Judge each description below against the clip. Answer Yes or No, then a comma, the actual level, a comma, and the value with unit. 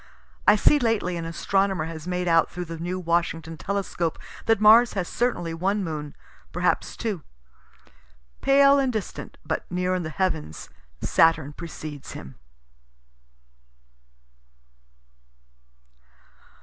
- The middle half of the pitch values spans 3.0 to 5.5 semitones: Yes, average, 3.8 semitones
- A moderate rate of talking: No, slow, 115 wpm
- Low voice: No, medium, 180 Hz